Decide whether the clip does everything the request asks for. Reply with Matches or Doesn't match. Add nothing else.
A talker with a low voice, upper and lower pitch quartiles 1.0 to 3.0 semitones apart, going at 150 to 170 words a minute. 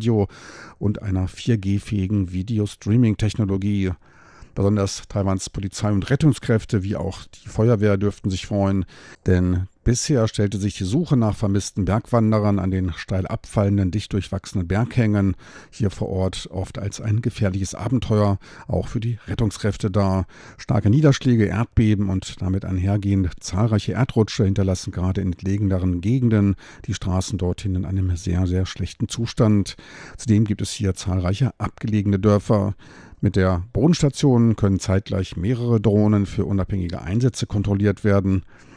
Doesn't match